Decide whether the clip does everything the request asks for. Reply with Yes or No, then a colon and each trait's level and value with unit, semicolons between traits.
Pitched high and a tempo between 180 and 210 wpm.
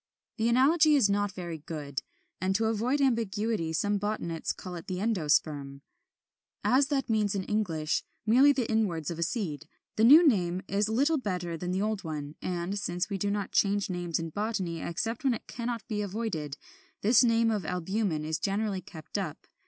Yes: high, 200 Hz; average, 185 wpm